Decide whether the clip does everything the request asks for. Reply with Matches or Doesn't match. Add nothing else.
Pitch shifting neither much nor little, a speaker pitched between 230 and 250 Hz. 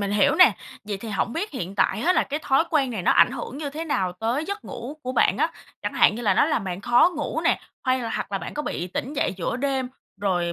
Doesn't match